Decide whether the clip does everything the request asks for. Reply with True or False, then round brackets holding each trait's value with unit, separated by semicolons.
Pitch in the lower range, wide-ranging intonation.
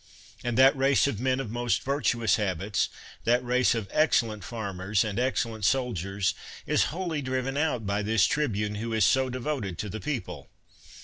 False (115 Hz; 4.2 semitones)